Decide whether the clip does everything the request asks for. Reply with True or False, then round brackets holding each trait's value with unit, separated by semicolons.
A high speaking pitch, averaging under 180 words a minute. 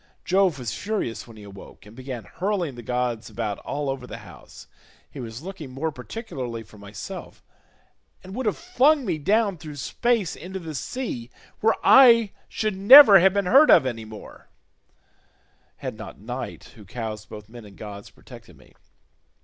False (145 Hz; 170 wpm)